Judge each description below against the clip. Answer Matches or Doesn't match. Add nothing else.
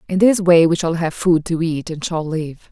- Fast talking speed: Matches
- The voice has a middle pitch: Matches